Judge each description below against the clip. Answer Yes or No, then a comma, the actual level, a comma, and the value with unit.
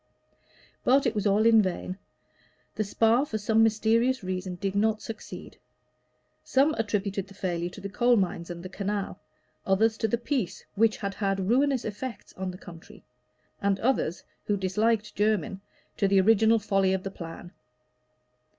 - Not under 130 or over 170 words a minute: Yes, average, 160 wpm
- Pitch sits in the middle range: No, high, 205 Hz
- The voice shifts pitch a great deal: No, average, 2.8 semitones